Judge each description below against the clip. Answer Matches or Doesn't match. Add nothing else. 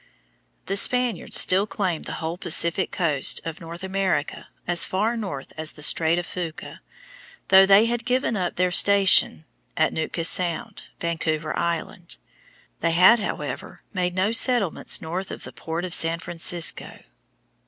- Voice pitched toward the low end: Doesn't match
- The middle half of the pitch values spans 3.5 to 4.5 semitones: Doesn't match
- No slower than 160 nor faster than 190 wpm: Doesn't match